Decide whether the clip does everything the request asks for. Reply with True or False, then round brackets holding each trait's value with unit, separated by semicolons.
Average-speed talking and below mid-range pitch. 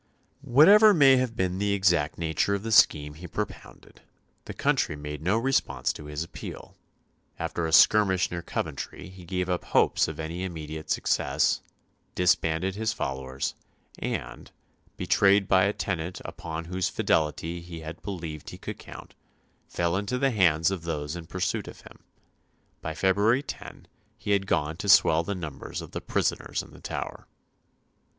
True (160 wpm; 90 Hz)